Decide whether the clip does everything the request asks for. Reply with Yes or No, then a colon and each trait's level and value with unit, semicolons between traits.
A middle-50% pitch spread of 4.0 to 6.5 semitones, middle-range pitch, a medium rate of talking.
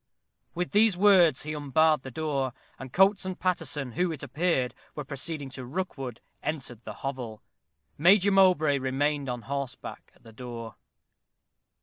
Yes: average, 5.3 semitones; medium, 145 Hz; average, 145 wpm